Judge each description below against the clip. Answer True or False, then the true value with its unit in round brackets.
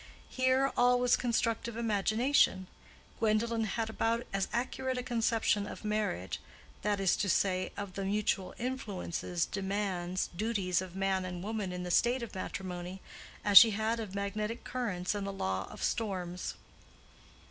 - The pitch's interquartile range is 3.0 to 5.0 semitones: True (3.6 semitones)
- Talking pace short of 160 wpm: True (145 wpm)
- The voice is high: True (205 Hz)